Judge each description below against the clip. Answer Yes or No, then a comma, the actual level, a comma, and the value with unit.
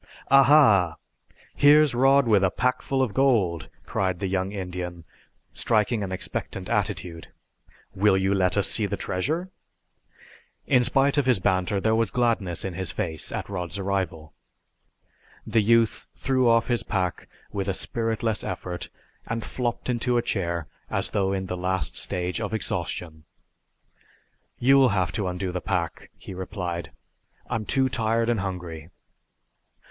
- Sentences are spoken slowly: No, average, 145 wpm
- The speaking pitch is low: Yes, low, 100 Hz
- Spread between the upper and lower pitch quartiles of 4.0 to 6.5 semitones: Yes, average, 4.4 semitones